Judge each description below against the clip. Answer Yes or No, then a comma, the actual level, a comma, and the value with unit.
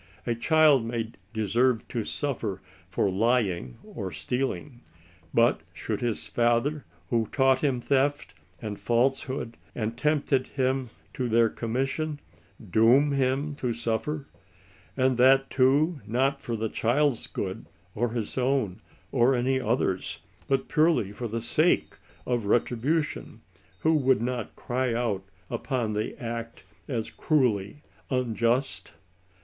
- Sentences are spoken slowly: Yes, slow, 130 wpm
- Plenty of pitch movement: No, average, 3.1 semitones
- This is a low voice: Yes, low, 125 Hz